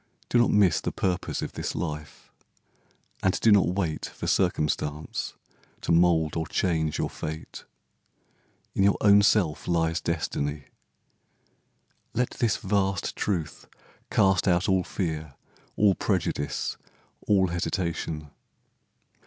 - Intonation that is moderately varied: Yes, average, 3.8 semitones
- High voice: No, very low, 85 Hz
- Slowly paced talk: Yes, slow, 120 wpm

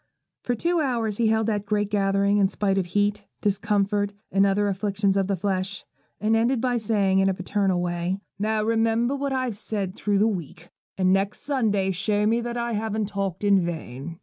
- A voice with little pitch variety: Yes, narrow, 2.3 semitones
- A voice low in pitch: No, high, 205 Hz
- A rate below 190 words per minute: No, average, 195 wpm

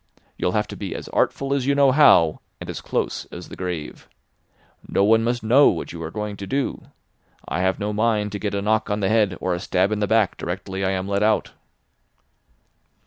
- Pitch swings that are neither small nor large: Yes, average, 3.0 semitones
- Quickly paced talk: Yes, fast, 220 wpm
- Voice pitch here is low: Yes, low, 105 Hz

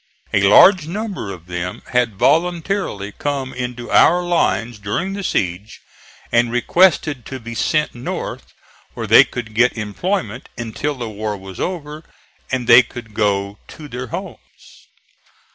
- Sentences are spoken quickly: No, average, 145 wpm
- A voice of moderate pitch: No, low, 120 Hz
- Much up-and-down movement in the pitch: Yes, wide, 6.5 semitones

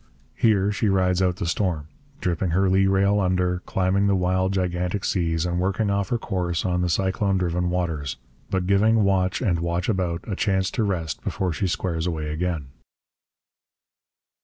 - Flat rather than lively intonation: Yes, narrow, 1.9 semitones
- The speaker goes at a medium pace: Yes, average, 170 wpm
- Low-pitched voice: Yes, very low, 90 Hz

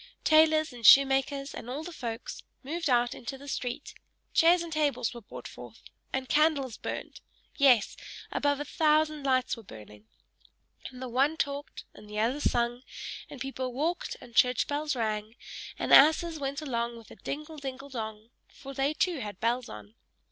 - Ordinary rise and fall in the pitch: Yes, average, 4.0 semitones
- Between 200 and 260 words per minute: No, average, 170 wpm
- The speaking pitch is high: Yes, very high, 270 Hz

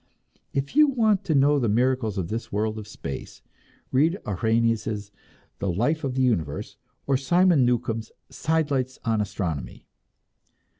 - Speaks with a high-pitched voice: No, low, 120 Hz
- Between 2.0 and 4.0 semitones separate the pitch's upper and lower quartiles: No, average, 5.2 semitones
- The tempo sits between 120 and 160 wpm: Yes, average, 140 wpm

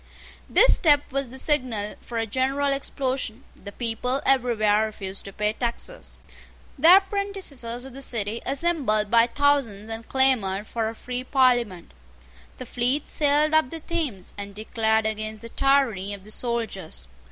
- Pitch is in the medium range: No, high, 240 Hz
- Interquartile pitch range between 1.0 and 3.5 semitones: No, average, 4.1 semitones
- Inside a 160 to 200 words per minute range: No, average, 150 wpm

